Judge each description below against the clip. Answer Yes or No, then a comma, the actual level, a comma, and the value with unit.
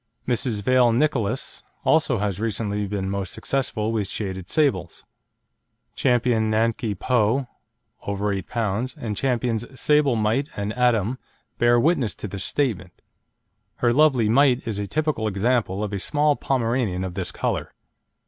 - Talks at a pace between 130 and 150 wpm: Yes, average, 140 wpm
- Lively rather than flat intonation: No, average, 4.0 semitones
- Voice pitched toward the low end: Yes, low, 115 Hz